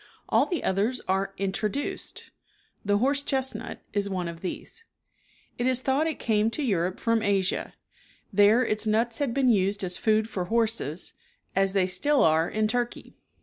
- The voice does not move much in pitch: No, average, 4.2 semitones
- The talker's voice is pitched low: No, high, 215 Hz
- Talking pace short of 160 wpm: No, average, 165 wpm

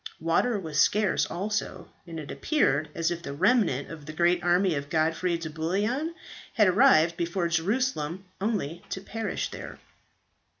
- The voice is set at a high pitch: No, medium, 175 Hz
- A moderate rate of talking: Yes, average, 155 wpm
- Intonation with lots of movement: No, average, 4.5 semitones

